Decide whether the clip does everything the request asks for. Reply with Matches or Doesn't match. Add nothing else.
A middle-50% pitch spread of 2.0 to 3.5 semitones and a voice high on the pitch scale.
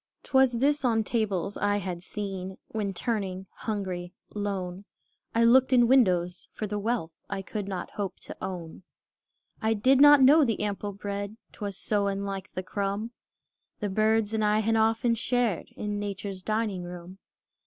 Matches